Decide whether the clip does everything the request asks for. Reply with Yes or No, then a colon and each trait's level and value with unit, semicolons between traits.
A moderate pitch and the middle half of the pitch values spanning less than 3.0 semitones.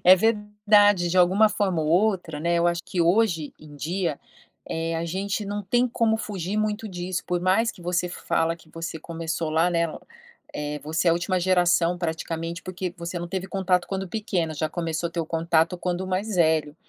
Yes: medium, 175 Hz; narrow, 2.6 semitones